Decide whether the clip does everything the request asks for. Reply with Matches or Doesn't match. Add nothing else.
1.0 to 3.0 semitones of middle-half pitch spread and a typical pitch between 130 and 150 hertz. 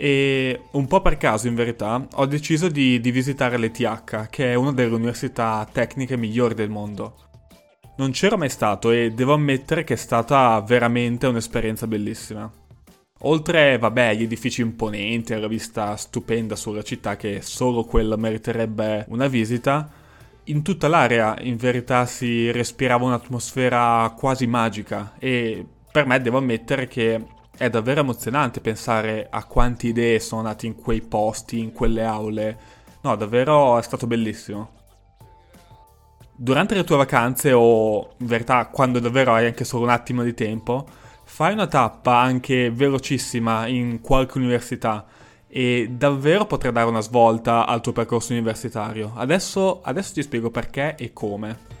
Doesn't match